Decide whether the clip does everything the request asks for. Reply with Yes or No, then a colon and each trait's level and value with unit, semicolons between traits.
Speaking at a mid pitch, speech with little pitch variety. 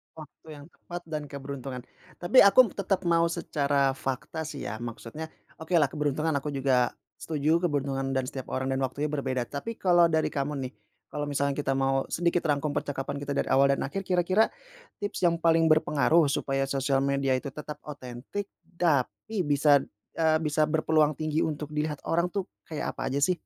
No: medium, 150 Hz; average, 3.1 semitones